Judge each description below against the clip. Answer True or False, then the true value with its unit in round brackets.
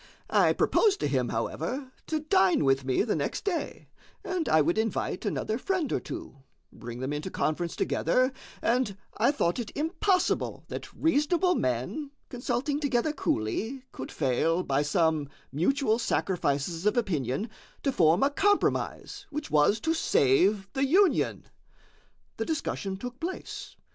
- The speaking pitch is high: True (215 Hz)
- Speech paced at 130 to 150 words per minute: True (145 wpm)